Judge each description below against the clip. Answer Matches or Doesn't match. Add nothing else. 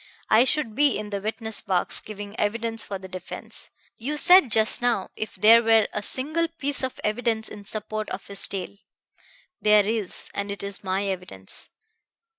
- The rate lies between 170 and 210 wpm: Matches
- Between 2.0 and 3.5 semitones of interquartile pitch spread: Matches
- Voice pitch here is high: Matches